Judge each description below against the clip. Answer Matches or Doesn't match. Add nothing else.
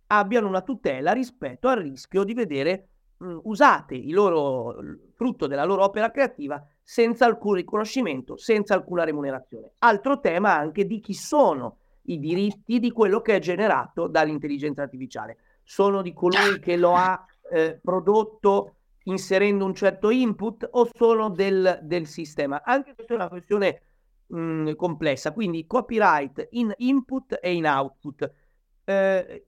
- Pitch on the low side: Doesn't match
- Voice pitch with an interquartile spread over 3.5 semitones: Matches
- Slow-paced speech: Doesn't match